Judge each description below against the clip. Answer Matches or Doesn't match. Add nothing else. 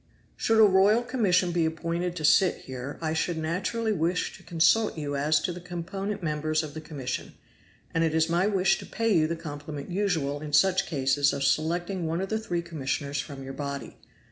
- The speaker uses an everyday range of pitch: Matches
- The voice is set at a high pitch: Doesn't match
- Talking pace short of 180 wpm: Doesn't match